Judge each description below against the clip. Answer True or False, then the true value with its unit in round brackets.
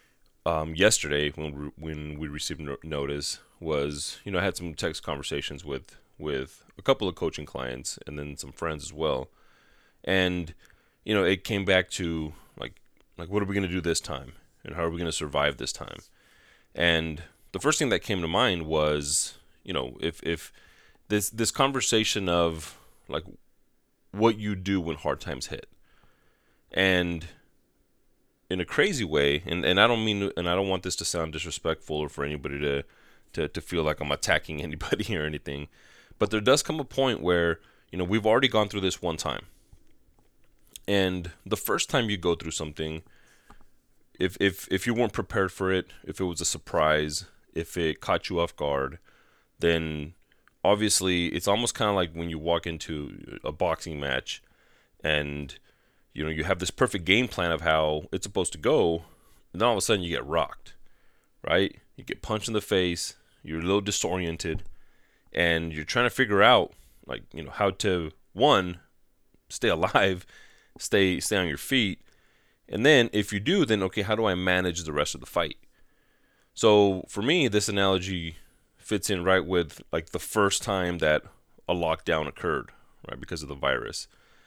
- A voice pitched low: True (85 Hz)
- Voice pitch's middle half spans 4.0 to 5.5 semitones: True (4.3 semitones)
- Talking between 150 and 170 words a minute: False (185 wpm)